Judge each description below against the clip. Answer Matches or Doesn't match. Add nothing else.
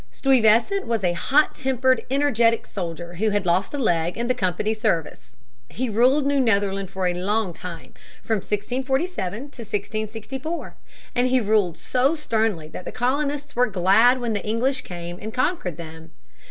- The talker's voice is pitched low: Doesn't match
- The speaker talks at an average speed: Matches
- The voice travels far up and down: Matches